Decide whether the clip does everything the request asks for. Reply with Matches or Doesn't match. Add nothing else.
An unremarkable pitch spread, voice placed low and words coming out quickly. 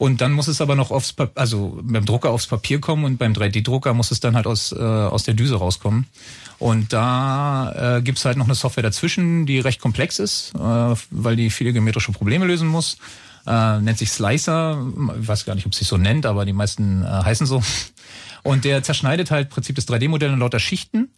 Matches